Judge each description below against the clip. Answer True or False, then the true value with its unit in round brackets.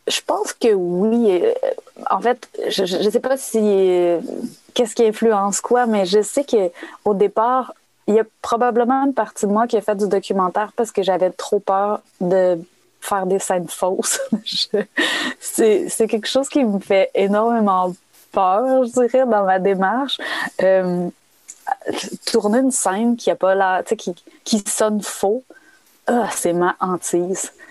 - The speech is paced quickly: False (165 wpm)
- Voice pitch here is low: False (215 Hz)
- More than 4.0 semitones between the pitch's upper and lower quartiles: True (4.5 semitones)